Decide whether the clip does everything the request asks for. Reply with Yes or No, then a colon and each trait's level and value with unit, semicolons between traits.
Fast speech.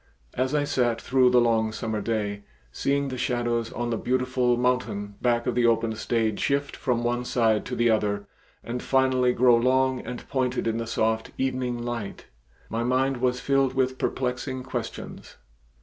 No: average, 170 wpm